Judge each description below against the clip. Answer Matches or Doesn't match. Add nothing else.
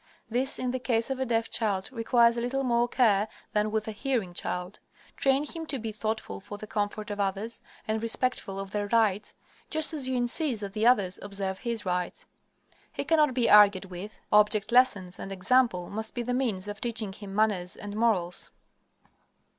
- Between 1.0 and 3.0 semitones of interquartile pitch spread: Doesn't match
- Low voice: Doesn't match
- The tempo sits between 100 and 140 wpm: Doesn't match